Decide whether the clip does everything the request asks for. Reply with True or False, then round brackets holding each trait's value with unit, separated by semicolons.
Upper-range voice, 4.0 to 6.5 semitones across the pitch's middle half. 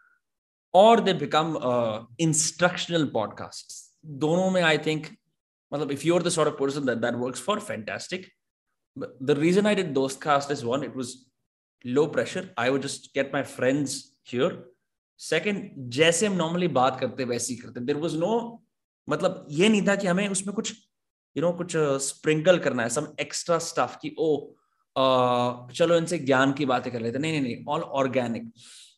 False (150 Hz; 5.2 semitones)